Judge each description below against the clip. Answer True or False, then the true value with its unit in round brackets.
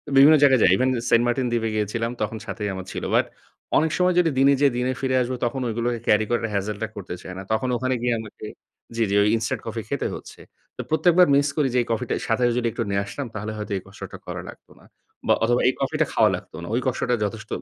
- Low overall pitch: True (120 Hz)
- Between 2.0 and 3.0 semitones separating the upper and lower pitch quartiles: False (3.4 semitones)